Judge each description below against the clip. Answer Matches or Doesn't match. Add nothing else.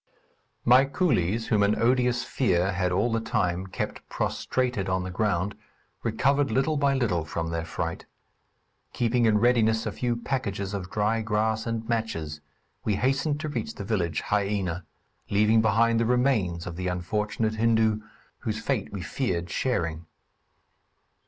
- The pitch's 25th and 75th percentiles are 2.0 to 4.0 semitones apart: Doesn't match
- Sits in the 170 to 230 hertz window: Doesn't match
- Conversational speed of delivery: Matches